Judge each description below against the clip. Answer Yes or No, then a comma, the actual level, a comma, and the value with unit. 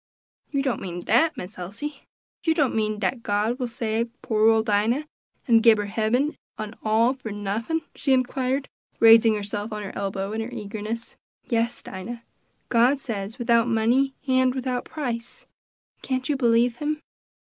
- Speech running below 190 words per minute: Yes, average, 165 wpm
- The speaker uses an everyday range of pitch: Yes, average, 3.2 semitones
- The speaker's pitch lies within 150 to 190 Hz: No, high, 230 Hz